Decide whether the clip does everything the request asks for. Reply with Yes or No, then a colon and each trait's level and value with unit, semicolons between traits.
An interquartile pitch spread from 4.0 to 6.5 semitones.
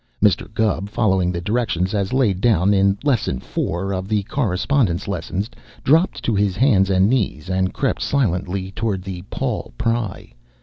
No: average, 3.3 semitones